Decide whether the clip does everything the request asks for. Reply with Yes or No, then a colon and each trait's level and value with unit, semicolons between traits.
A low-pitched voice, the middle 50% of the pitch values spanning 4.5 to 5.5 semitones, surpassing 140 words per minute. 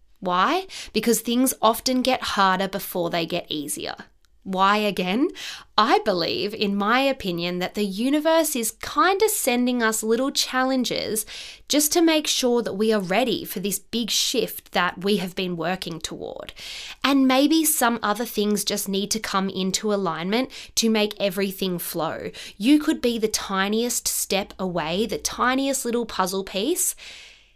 No: high, 220 Hz; average, 4.8 semitones; average, 155 wpm